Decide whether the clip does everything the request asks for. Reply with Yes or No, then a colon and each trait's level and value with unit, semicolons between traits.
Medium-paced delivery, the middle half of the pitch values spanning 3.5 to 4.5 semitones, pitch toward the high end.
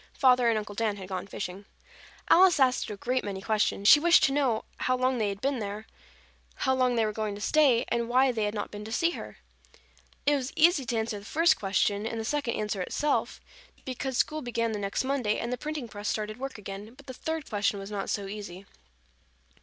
No: fast, 225 wpm; average, 4.2 semitones; high, 230 Hz